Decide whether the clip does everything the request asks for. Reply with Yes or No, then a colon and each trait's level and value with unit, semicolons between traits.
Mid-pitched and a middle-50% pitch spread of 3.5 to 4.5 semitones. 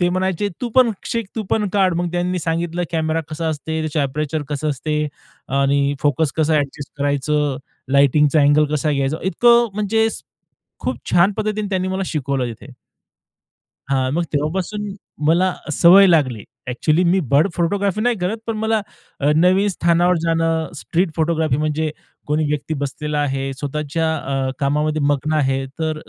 Yes: medium, 160 Hz; average, 3.9 semitones